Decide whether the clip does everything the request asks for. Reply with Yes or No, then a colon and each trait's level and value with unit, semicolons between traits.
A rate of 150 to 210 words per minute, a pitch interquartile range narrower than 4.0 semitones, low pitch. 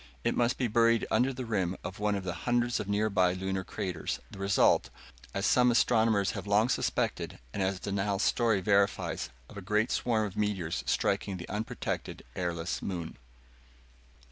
Yes: average, 170 wpm; average, 3.2 semitones; low, 100 Hz